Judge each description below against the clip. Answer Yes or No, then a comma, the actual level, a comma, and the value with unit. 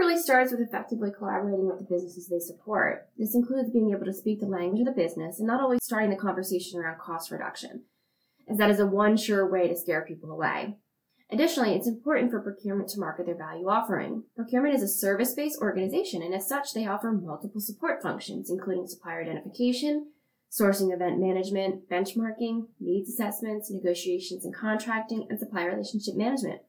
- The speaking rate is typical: Yes, average, 180 wpm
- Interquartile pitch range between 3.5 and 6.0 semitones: Yes, average, 3.8 semitones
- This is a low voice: No, high, 205 Hz